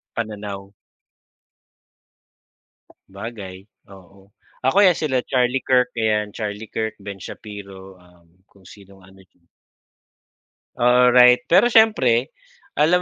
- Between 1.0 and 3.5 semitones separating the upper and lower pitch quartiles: No, average, 4.3 semitones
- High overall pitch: No, low, 105 Hz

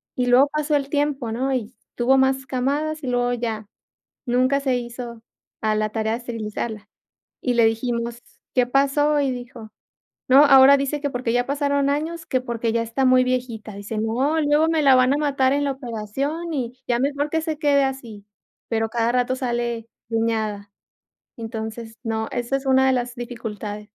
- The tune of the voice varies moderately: Yes, average, 3.3 semitones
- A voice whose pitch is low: No, very high, 250 Hz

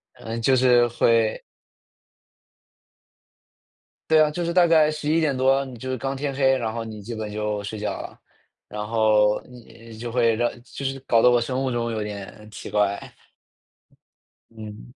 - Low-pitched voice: Yes, low, 115 Hz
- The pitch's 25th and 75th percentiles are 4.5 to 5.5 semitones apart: No, average, 3.6 semitones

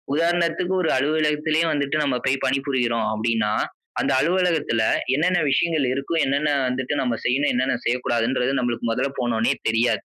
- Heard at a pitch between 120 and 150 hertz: Yes, low, 135 Hz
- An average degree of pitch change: Yes, average, 4.3 semitones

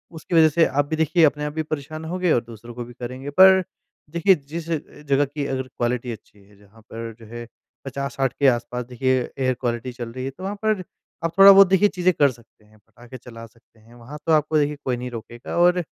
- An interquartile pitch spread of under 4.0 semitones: No, average, 5.1 semitones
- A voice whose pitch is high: No, low, 135 Hz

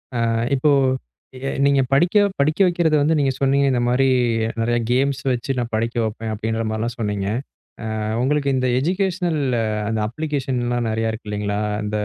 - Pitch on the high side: No, low, 130 Hz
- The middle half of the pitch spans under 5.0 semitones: Yes, average, 4.3 semitones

